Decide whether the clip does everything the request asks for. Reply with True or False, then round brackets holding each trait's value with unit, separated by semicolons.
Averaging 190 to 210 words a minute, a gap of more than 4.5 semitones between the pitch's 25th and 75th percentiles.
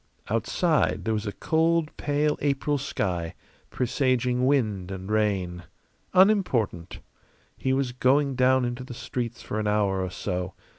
False (140 wpm; 5.2 semitones)